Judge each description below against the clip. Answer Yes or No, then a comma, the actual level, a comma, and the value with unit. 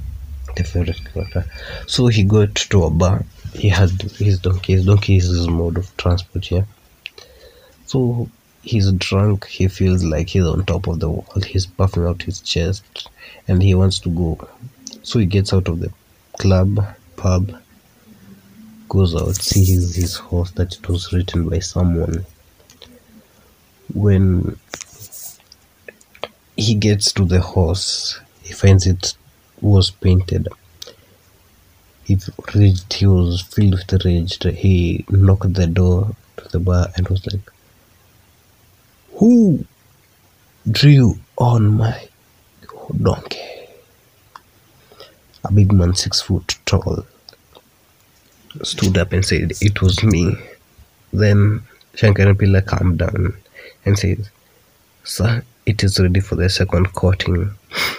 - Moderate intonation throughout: No, narrow, 2.3 semitones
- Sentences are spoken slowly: No, average, 125 wpm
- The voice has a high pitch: No, very low, 95 Hz